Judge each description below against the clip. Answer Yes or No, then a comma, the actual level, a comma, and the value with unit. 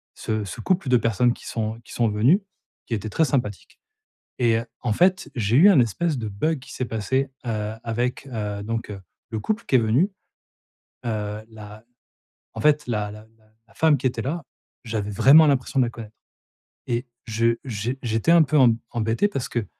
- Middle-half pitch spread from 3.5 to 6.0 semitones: Yes, average, 3.9 semitones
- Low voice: Yes, low, 115 Hz